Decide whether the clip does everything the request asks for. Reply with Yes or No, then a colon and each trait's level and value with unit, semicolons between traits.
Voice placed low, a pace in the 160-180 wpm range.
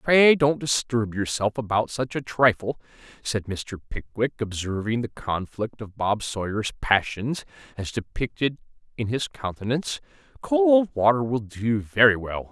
No: low, 120 Hz; average, 140 wpm